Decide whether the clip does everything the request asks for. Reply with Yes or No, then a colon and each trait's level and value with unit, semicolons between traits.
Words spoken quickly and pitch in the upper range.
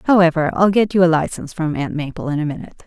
No: fast, 250 wpm; medium, 165 Hz